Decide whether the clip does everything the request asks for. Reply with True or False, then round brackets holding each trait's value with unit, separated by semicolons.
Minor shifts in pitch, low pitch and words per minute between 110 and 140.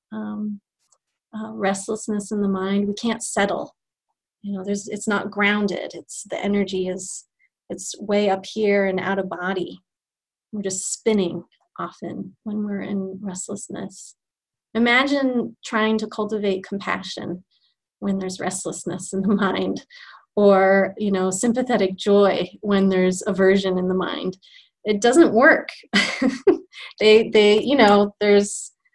False (2.1 semitones; 205 Hz; 135 wpm)